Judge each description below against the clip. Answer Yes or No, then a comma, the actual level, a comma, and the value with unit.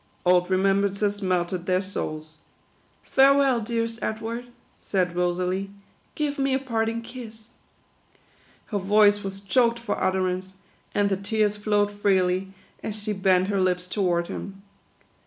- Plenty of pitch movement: No, average, 3.1 semitones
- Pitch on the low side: No, high, 200 Hz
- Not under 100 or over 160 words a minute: Yes, average, 140 wpm